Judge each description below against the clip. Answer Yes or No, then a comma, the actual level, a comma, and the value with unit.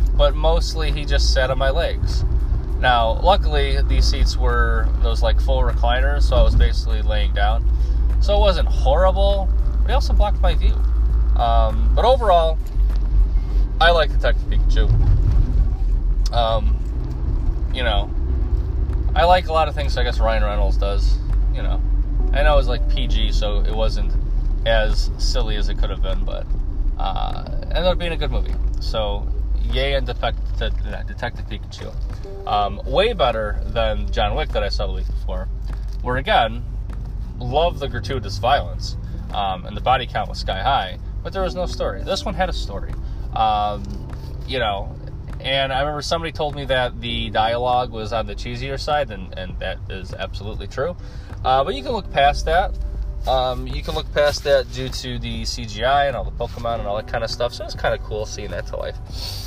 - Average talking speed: Yes, average, 190 wpm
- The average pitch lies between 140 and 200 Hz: No, low, 105 Hz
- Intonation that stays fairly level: No, average, 4.4 semitones